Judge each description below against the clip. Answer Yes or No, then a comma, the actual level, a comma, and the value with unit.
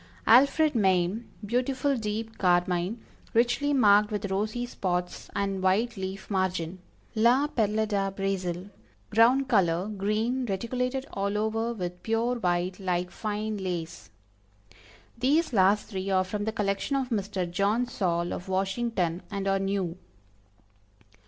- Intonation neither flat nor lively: Yes, average, 3.7 semitones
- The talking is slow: Yes, slow, 130 wpm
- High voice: Yes, high, 205 Hz